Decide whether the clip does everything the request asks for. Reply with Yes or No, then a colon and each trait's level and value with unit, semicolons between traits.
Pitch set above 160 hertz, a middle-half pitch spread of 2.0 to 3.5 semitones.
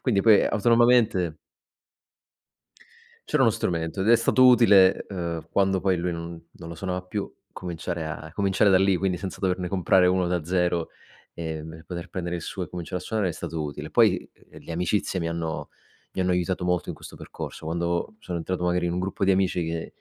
No: very low, 90 Hz; narrow, 2.4 semitones